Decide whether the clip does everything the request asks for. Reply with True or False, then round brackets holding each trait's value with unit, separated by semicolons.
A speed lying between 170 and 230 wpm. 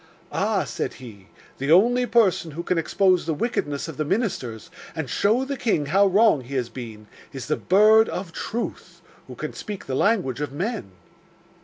True (180 wpm)